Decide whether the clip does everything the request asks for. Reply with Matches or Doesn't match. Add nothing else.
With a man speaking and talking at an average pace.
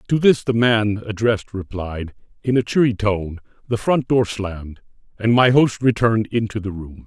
Matches